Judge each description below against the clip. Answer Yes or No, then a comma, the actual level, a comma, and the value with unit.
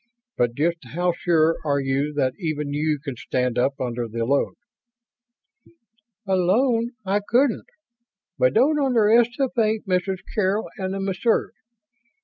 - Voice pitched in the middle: Yes, medium, 180 Hz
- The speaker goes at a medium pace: No, slow, 125 wpm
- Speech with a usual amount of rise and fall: No, wide, 7.6 semitones